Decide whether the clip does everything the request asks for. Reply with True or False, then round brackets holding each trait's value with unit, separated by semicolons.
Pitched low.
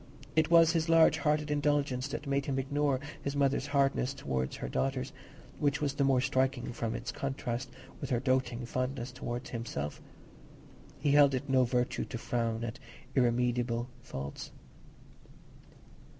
True (130 Hz)